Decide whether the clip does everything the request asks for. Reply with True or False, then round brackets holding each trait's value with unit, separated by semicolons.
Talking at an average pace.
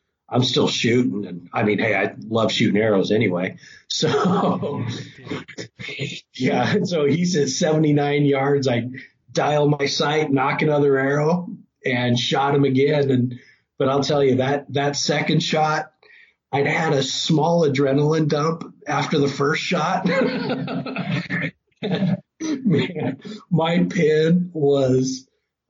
False (125 wpm)